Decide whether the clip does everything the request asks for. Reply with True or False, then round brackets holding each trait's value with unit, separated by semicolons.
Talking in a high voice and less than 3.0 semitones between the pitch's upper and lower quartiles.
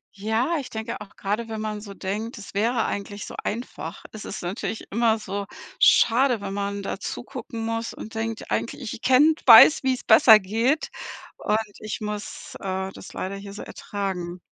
True (215 Hz; 2.4 semitones)